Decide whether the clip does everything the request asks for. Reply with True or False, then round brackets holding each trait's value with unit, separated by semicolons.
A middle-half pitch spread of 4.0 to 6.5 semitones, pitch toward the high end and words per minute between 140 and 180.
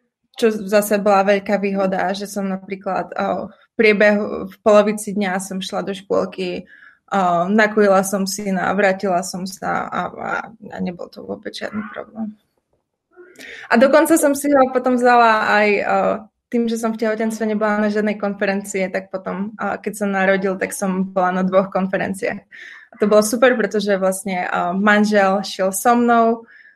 False (2.7 semitones; 205 Hz; 160 wpm)